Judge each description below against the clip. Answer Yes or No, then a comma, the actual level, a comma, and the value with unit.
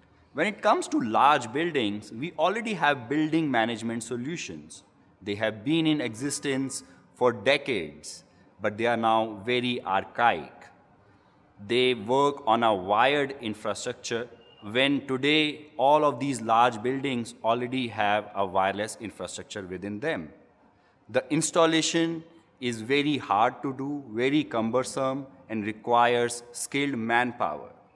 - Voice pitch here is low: Yes, low, 125 Hz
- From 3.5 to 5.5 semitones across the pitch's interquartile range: Yes, average, 4.2 semitones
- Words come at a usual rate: No, slow, 125 wpm